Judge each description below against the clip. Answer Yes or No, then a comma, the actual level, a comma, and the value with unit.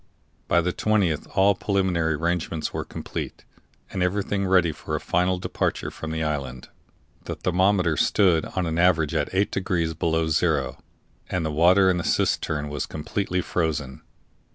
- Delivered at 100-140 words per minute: No, average, 155 wpm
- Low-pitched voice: Yes, very low, 85 Hz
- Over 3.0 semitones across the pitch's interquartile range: No, average, 2.7 semitones